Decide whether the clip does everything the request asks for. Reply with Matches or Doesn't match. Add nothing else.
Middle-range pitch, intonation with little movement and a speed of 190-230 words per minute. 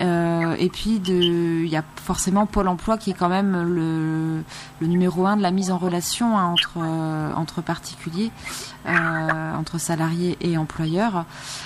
Doesn't match